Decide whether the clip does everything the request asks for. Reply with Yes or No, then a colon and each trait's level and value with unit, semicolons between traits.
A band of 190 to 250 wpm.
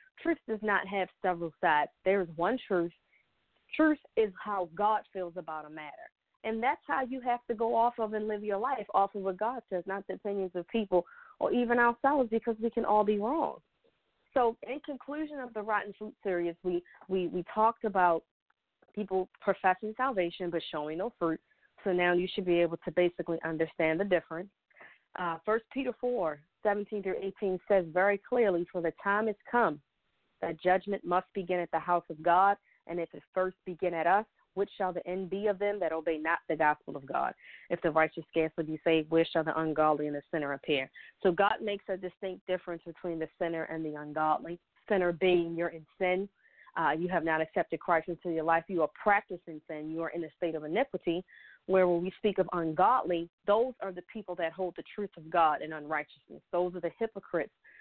Yes: fast, 205 wpm